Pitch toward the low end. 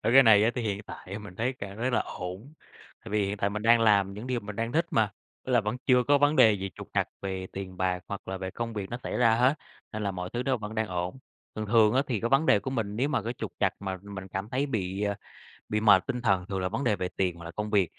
Yes: low, 105 Hz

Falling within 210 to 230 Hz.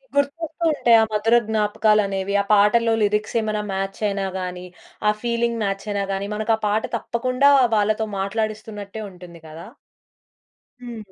Yes: high, 215 Hz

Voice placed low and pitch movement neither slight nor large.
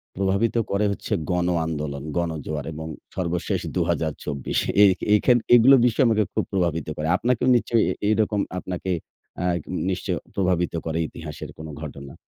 Yes: very low, 90 Hz; average, 5.0 semitones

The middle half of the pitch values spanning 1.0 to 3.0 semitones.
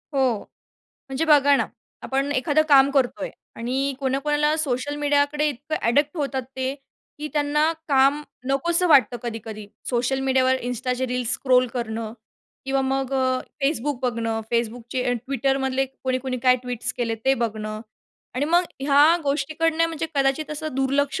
Yes: narrow, 2.6 semitones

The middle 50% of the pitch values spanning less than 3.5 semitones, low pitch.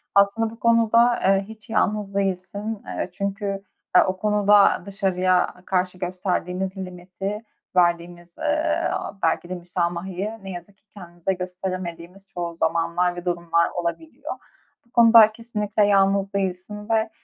No: average, 2.7 semitones; high, 190 Hz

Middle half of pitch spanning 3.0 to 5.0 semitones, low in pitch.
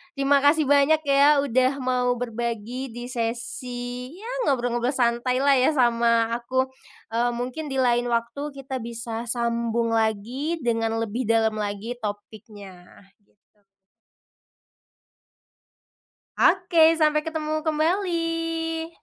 No: average, 3.7 semitones; high, 245 Hz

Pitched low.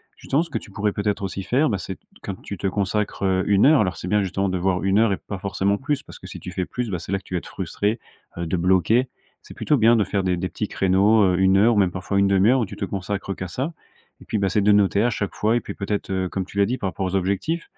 Yes: low, 100 Hz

